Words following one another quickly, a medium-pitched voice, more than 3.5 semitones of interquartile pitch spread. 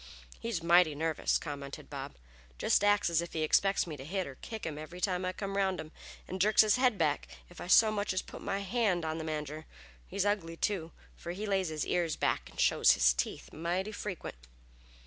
Yes: fast, 215 wpm; medium, 180 Hz; average, 4.0 semitones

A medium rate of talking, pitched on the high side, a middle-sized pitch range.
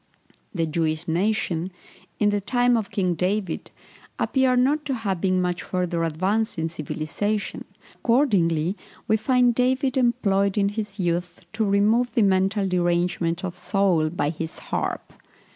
Yes: average, 145 wpm; high, 195 Hz; average, 4.3 semitones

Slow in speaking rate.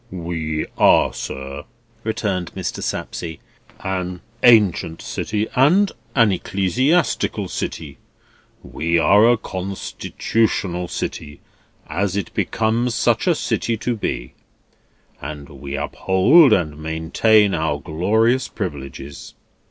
Yes: slow, 105 wpm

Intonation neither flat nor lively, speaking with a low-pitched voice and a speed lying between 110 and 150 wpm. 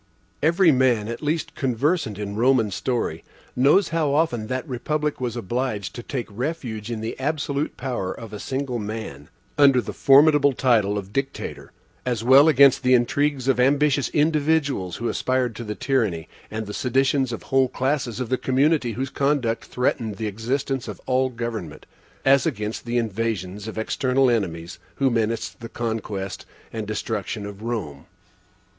No: average, 3.8 semitones; low, 125 Hz; average, 160 wpm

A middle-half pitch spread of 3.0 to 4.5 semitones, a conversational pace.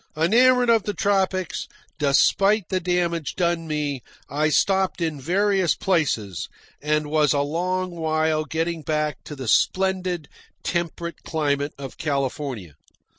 No: average, 3.9 semitones; slow, 125 wpm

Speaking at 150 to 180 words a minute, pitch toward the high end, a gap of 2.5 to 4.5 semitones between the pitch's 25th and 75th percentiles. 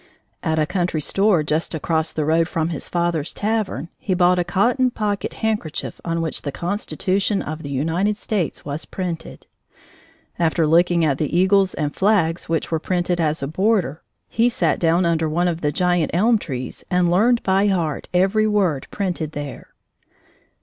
No: average, 170 wpm; medium, 175 Hz; average, 3.6 semitones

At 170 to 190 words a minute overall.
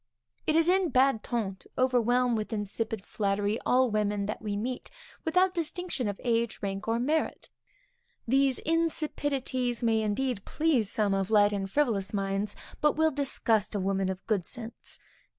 No: average, 160 wpm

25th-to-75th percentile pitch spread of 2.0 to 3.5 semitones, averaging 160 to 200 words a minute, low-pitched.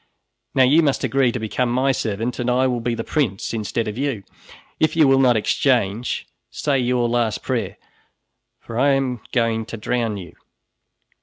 Yes: average, 2.8 semitones; average, 175 wpm; low, 125 Hz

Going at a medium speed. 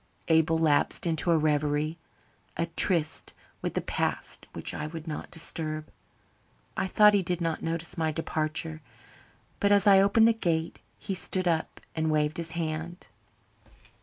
Yes: average, 155 wpm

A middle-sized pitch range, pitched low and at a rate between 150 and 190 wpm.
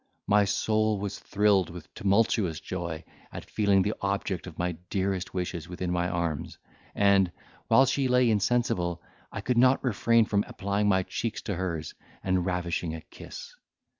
Yes: average, 3.1 semitones; very low, 95 Hz; average, 160 wpm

